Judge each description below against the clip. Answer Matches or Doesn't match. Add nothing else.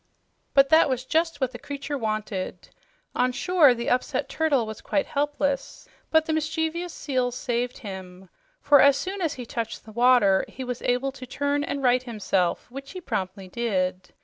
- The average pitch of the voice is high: Matches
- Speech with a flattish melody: Doesn't match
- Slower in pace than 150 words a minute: Doesn't match